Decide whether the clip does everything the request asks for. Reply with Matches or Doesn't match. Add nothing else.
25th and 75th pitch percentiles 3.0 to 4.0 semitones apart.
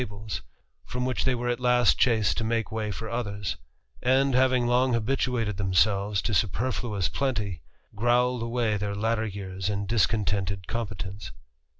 Matches